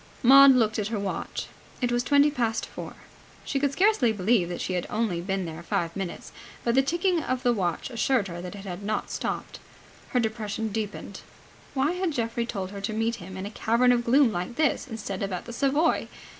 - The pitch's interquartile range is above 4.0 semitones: Yes, average, 4.7 semitones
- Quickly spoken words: Yes, fast, 210 wpm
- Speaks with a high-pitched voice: Yes, high, 225 Hz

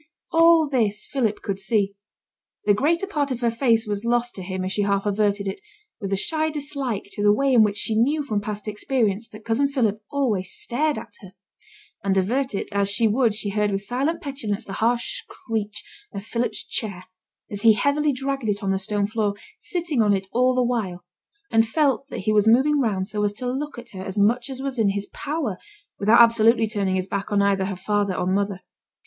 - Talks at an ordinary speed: No, fast, 215 wpm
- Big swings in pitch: No, average, 4.3 semitones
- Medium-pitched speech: No, high, 220 Hz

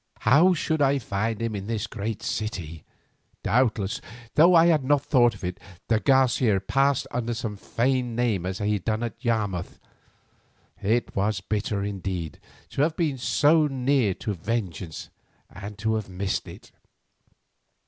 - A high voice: No, low, 115 Hz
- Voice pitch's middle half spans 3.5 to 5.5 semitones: Yes, average, 4.9 semitones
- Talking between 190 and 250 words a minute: No, average, 155 wpm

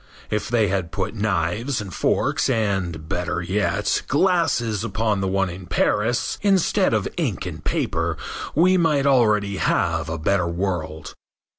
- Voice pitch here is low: Yes, low, 100 Hz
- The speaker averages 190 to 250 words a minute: No, average, 145 wpm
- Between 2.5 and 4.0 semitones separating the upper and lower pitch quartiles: No, average, 4.7 semitones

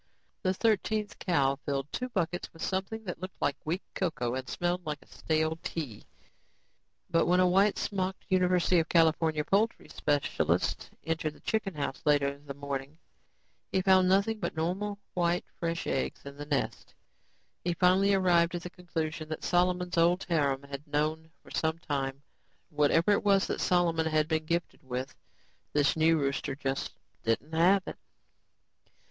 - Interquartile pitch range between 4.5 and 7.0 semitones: No, average, 3.9 semitones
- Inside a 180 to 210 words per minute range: No, average, 160 wpm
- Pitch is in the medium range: Yes, medium, 165 Hz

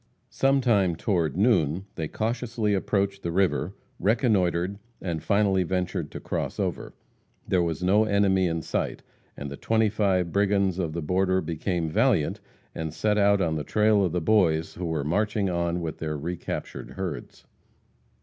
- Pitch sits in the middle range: No, very low, 95 Hz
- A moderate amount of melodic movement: Yes, average, 3.5 semitones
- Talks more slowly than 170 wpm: Yes, average, 160 wpm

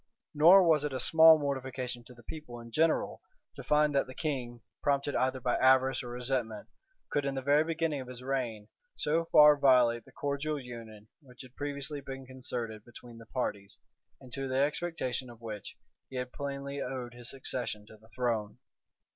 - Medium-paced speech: Yes, average, 185 wpm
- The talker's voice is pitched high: No, low, 130 Hz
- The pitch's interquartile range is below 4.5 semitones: Yes, average, 2.9 semitones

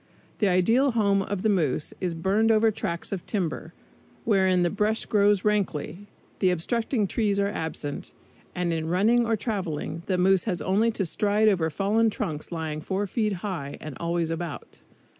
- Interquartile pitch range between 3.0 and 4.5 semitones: Yes, average, 3.9 semitones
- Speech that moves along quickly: No, average, 170 wpm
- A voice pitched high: Yes, high, 195 Hz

